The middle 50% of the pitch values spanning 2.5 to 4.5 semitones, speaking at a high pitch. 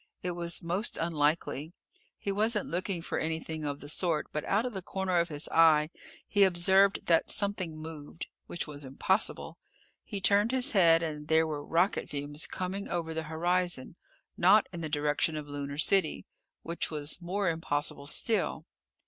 No: average, 3.8 semitones; medium, 165 Hz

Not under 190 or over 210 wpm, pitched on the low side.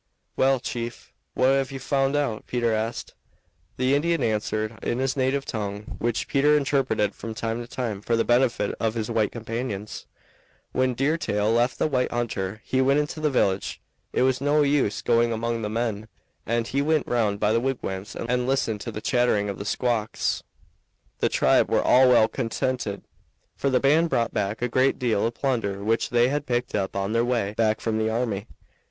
Yes: average, 195 wpm; low, 120 Hz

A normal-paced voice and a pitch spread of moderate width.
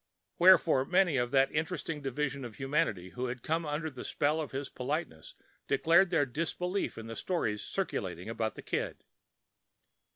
Yes: average, 160 wpm; average, 4.4 semitones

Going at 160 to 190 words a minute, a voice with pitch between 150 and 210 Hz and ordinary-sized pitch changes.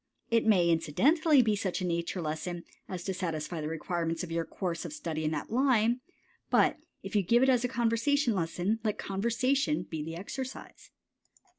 No: average, 180 wpm; high, 190 Hz; wide, 6.2 semitones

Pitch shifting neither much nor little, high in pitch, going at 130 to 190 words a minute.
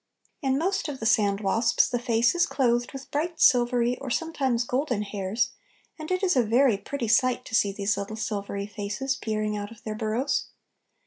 Yes: average, 4.2 semitones; high, 235 Hz; average, 185 wpm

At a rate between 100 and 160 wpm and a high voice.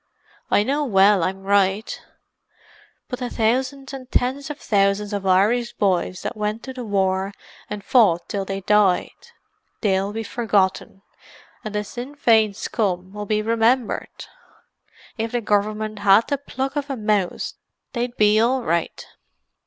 Yes: average, 145 wpm; high, 210 Hz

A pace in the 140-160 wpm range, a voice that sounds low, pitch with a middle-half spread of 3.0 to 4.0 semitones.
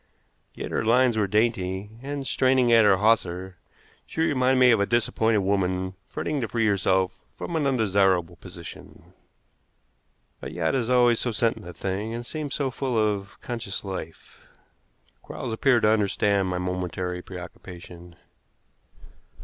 No: average, 145 wpm; low, 105 Hz; average, 4.4 semitones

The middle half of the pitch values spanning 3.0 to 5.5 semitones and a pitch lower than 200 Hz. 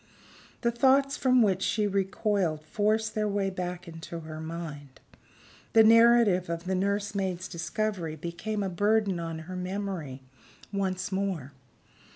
Yes: average, 3.9 semitones; high, 190 Hz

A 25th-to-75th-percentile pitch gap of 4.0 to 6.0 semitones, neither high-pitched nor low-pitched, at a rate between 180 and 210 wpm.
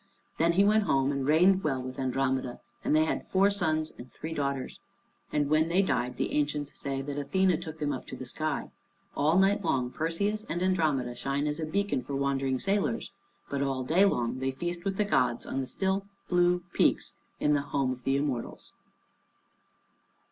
Yes: average, 4.9 semitones; medium, 150 Hz; average, 190 wpm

